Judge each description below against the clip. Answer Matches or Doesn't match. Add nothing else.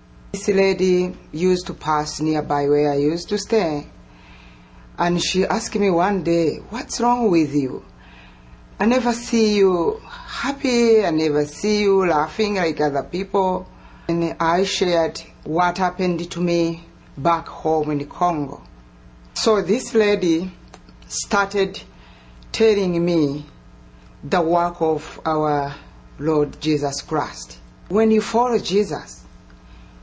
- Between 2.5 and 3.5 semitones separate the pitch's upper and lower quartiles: Doesn't match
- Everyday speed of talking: Doesn't match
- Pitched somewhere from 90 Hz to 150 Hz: Doesn't match